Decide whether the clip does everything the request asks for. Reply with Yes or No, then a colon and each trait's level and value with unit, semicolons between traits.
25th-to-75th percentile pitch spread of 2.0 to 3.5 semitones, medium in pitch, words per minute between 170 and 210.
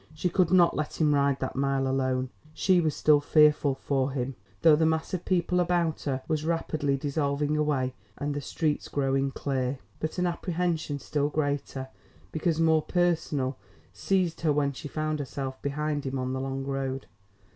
Yes: average, 2.9 semitones; medium, 145 Hz; average, 175 wpm